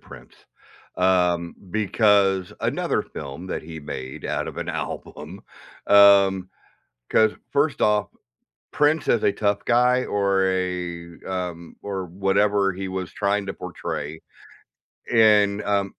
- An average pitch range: No, narrow, 2.3 semitones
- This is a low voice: Yes, very low, 95 Hz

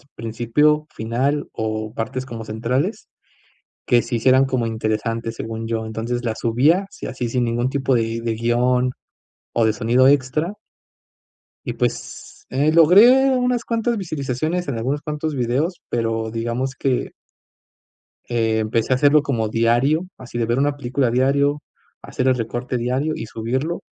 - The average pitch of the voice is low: Yes, low, 125 Hz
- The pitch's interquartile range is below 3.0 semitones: No, average, 3.9 semitones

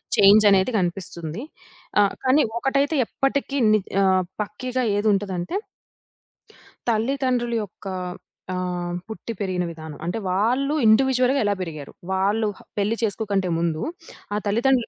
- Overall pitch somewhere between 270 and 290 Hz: No, high, 205 Hz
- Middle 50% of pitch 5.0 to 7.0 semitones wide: Yes, average, 5.3 semitones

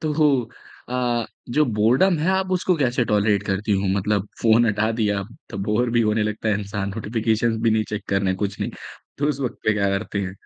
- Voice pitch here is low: Yes, low, 110 Hz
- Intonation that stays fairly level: No, average, 3.2 semitones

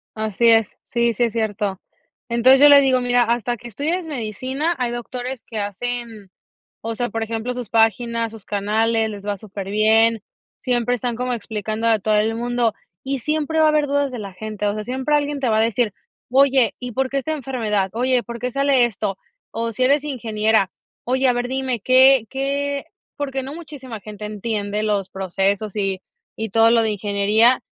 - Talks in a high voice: Yes, high, 235 Hz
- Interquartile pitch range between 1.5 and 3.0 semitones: No, average, 3.4 semitones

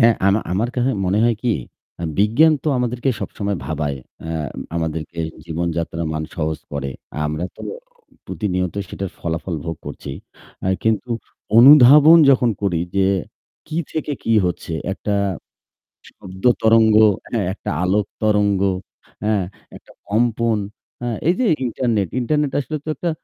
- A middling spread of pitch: No, wide, 5.9 semitones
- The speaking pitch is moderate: No, low, 105 Hz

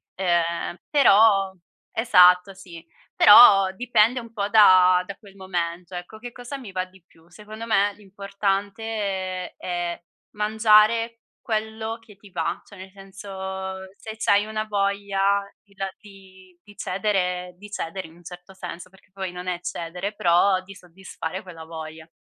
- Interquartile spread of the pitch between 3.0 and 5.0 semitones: No, narrow, 2.6 semitones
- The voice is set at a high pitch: Yes, high, 195 Hz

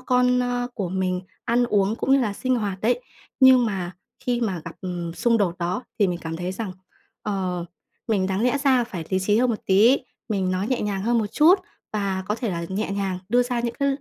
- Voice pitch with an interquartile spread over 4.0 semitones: Yes, average, 4.6 semitones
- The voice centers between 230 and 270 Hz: No, high, 210 Hz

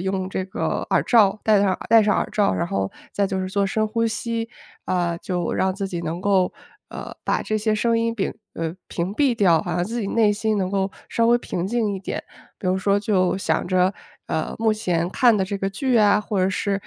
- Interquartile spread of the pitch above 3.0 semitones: No, average, 2.7 semitones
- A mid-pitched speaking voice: No, high, 195 Hz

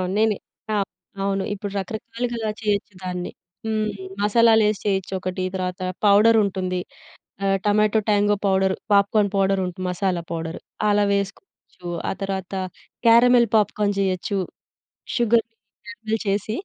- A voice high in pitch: Yes, high, 205 Hz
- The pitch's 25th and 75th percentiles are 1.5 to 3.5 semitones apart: Yes, narrow, 2.4 semitones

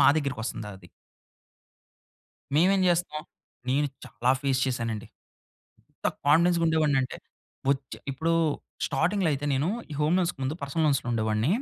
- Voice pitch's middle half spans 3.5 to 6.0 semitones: Yes, average, 4.1 semitones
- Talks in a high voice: No, medium, 140 Hz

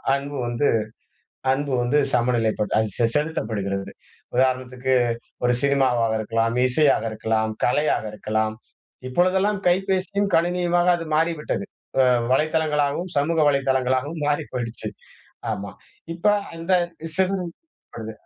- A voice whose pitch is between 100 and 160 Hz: Yes, medium, 140 Hz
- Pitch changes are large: Yes, wide, 6.0 semitones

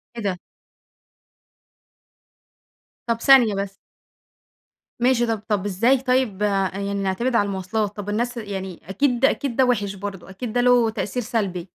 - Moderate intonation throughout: Yes, average, 3.6 semitones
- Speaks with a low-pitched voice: No, high, 210 Hz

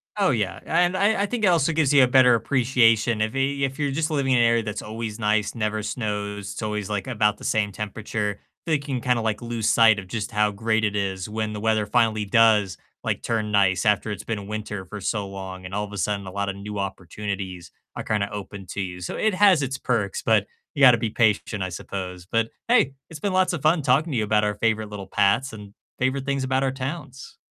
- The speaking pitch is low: Yes, low, 110 Hz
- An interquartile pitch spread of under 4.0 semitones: No, average, 4.3 semitones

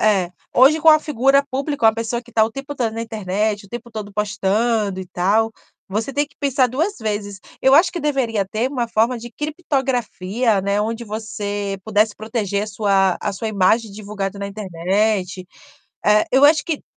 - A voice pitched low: No, high, 220 Hz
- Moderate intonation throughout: Yes, average, 4.0 semitones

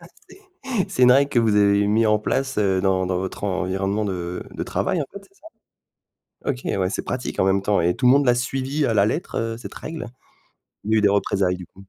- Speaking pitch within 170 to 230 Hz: No, low, 105 Hz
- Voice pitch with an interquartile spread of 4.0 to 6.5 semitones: Yes, average, 4.8 semitones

